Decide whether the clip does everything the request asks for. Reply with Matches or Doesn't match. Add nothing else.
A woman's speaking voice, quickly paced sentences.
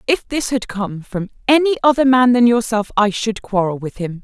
Matches